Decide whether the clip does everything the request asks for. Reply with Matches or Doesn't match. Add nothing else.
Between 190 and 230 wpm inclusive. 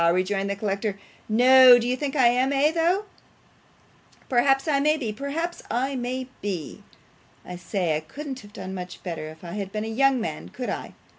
Matches